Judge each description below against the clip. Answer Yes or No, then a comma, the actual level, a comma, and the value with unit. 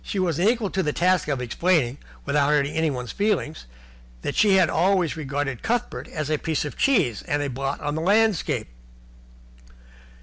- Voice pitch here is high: No, medium, 160 Hz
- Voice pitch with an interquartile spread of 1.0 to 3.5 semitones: No, average, 4.9 semitones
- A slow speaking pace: No, average, 170 wpm